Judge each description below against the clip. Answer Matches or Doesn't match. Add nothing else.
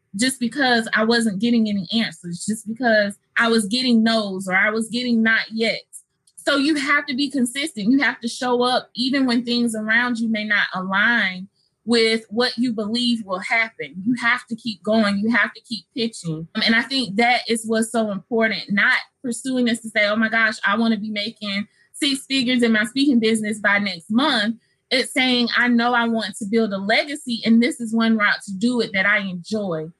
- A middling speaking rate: Doesn't match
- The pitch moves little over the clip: Matches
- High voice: Matches